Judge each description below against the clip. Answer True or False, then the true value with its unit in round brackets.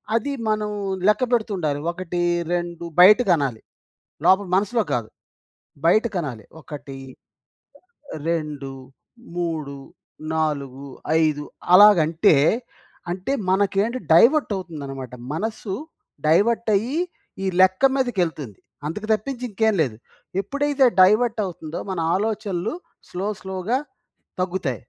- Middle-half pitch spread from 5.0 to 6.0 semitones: True (5.6 semitones)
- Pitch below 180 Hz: False (185 Hz)